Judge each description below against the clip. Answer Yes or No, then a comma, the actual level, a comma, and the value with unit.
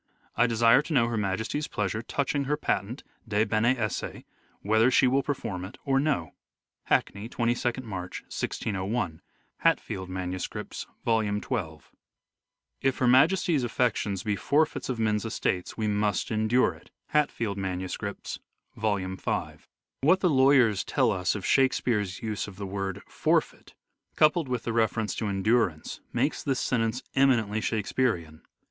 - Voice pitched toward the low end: Yes, low, 110 Hz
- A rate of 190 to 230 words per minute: No, average, 150 wpm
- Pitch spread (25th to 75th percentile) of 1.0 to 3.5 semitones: No, average, 4.3 semitones